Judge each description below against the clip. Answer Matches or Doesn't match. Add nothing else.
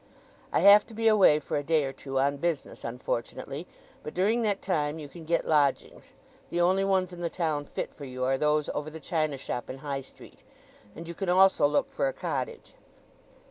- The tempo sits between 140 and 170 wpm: Doesn't match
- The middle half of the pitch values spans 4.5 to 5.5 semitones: Matches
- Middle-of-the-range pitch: Matches